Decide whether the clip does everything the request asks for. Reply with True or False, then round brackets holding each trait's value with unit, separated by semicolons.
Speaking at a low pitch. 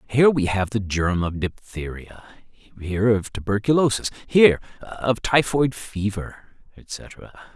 True (110 Hz)